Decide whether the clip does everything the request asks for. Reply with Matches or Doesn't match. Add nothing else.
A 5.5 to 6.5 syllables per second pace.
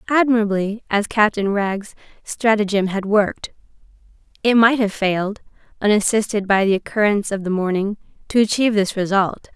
Matches